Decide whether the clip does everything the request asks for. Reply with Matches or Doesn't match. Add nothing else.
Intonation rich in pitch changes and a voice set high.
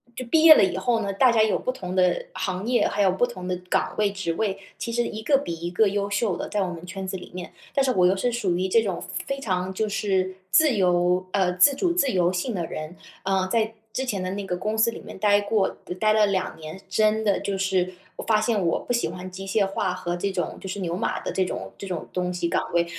Doesn't match